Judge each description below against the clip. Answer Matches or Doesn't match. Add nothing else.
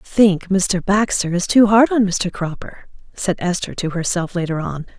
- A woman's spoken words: Matches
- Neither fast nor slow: Matches